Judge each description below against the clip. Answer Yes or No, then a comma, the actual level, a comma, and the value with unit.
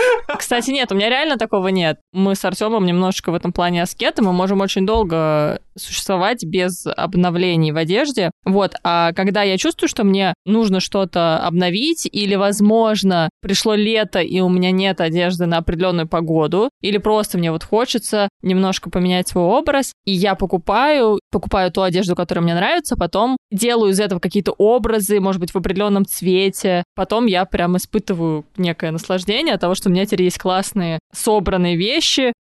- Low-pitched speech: No, high, 190 Hz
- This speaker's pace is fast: Yes, fast, 170 wpm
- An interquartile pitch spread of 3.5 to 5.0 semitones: No, average, 3.0 semitones